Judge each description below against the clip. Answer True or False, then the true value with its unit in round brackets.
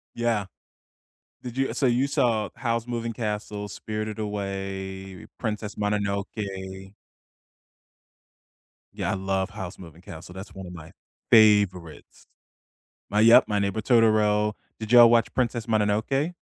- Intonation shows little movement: False (3.0 semitones)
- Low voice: True (105 Hz)